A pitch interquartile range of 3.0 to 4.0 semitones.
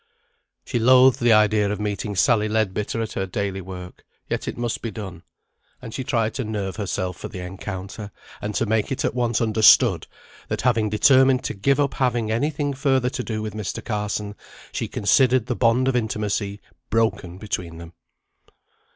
Yes: average, 3.3 semitones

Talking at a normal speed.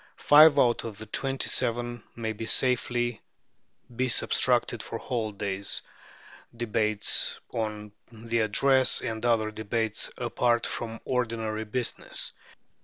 No: slow, 110 wpm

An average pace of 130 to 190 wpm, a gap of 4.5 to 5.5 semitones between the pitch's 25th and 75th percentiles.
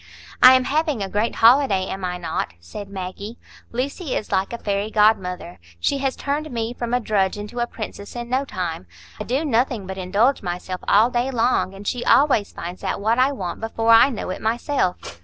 No: fast, 205 wpm; average, 4.8 semitones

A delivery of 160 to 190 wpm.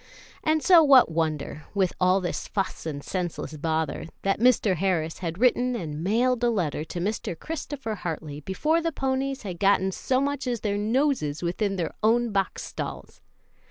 Yes: average, 170 wpm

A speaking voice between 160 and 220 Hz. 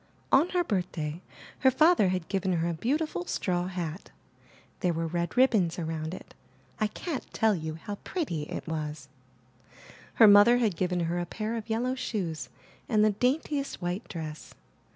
Yes: medium, 185 Hz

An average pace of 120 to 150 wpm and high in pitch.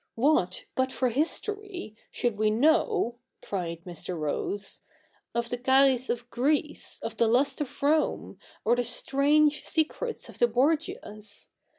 Yes: average, 145 wpm; very high, 255 Hz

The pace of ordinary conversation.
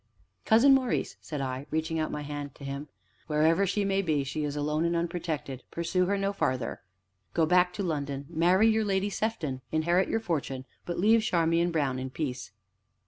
Yes: average, 185 wpm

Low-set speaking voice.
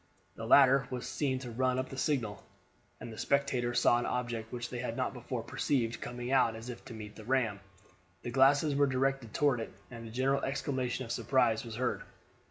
Yes: low, 125 Hz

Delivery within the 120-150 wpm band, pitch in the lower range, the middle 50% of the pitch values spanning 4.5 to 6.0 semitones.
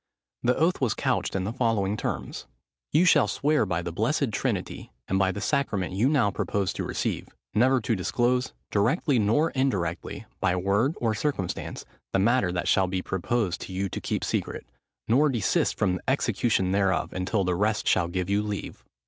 No: average, 180 wpm; low, 105 Hz; average, 5.1 semitones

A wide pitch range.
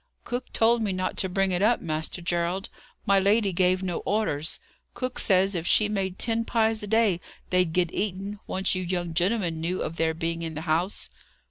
No: average, 3.4 semitones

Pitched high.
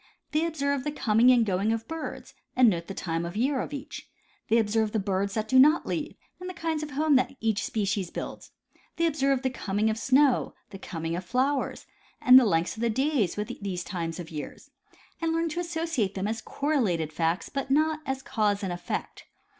Yes: high, 230 Hz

